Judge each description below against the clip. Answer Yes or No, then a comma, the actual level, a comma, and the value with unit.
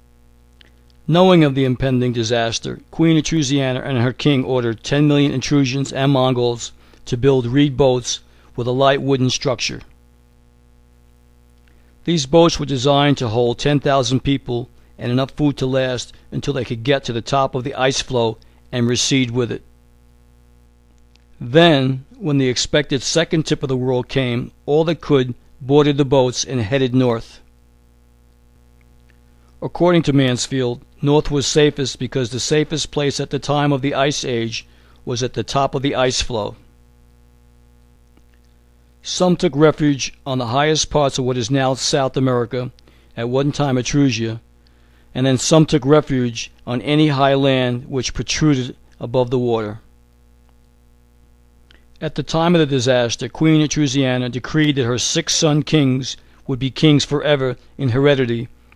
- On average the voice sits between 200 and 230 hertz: No, low, 130 Hz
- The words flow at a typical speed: Yes, average, 150 wpm